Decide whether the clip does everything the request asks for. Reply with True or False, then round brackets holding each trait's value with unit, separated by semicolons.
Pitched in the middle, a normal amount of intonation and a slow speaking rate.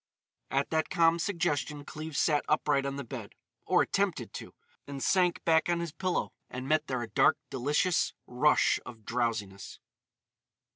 False (150 Hz; 4.2 semitones; 155 wpm)